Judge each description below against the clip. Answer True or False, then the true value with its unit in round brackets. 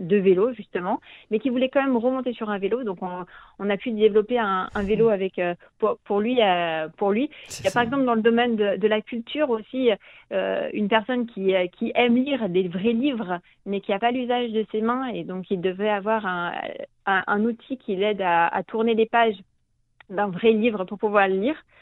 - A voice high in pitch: True (215 Hz)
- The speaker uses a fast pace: True (225 wpm)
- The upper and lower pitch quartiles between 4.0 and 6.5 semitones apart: False (3.5 semitones)